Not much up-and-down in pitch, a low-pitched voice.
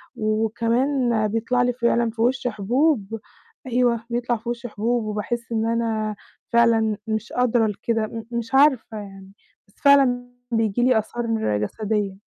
No: narrow, 2.1 semitones; high, 230 Hz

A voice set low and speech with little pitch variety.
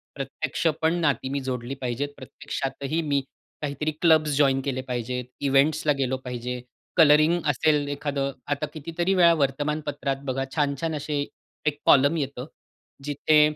No: medium, 145 Hz; narrow, 2.3 semitones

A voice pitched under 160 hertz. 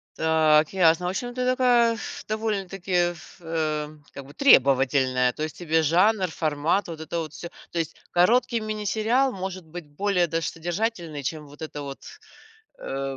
No: medium, 170 Hz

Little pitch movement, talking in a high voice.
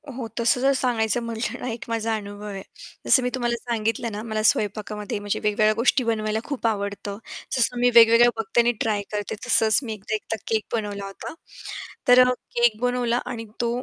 Yes: narrow, 2.2 semitones; high, 225 Hz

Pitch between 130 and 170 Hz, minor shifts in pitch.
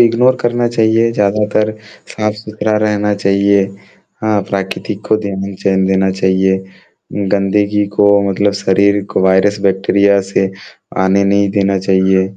No: low, 100 Hz; narrow, 1.7 semitones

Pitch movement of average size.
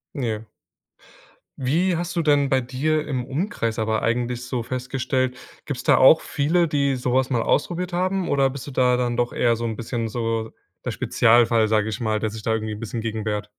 Yes: average, 3.8 semitones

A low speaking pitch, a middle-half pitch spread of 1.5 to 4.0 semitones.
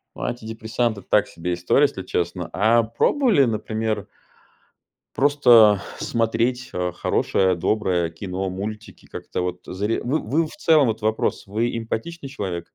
No: low, 110 Hz; average, 4.4 semitones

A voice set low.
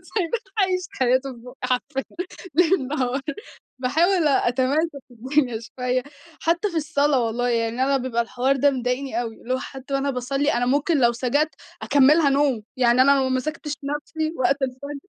No: very high, 270 Hz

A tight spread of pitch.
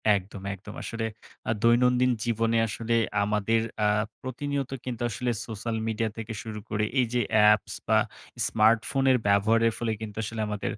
Yes: narrow, 2.0 semitones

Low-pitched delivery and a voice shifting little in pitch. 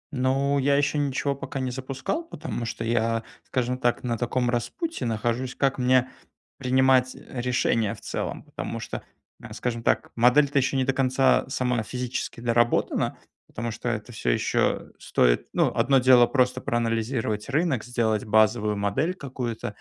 Yes: low, 125 Hz; narrow, 2.3 semitones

